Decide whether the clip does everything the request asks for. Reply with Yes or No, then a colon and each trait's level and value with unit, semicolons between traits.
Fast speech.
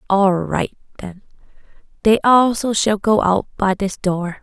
No: average, 150 wpm